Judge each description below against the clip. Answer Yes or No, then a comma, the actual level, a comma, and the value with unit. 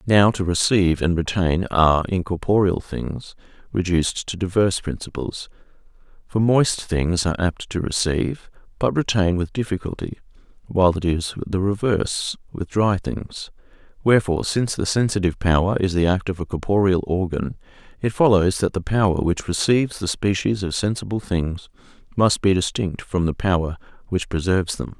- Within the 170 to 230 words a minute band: No, average, 155 wpm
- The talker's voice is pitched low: Yes, very low, 95 Hz